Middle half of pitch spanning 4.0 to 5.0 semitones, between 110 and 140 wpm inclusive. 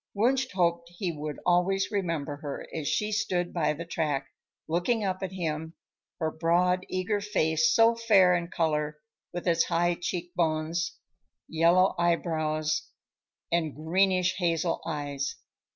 No: average, 2.7 semitones; slow, 135 wpm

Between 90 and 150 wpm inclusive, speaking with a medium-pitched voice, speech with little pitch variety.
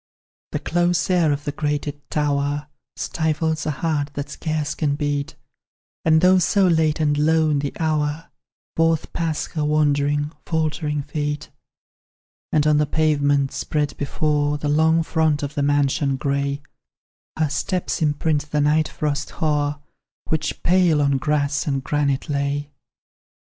Yes: average, 140 wpm; medium, 150 Hz; narrow, 1.6 semitones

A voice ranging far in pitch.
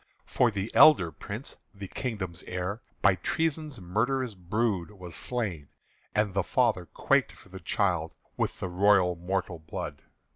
No: average, 4.0 semitones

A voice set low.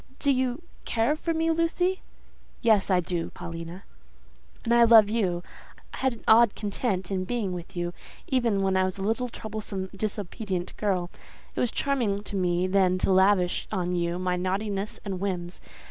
No: high, 200 Hz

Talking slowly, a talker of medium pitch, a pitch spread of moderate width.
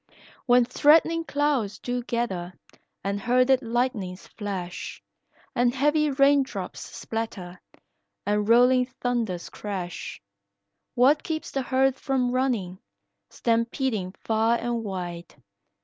No: slow, 105 wpm; high, 240 Hz; average, 4.6 semitones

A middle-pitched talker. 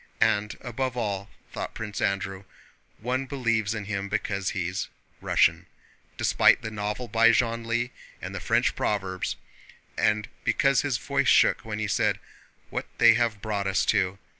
No: low, 110 Hz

